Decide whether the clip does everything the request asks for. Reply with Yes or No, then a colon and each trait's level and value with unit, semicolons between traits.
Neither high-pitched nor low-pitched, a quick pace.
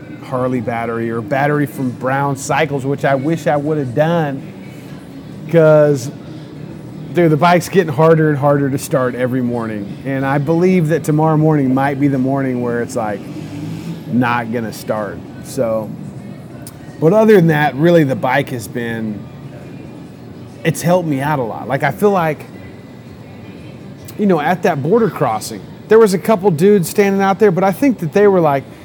No: medium, 150 Hz; average, 170 wpm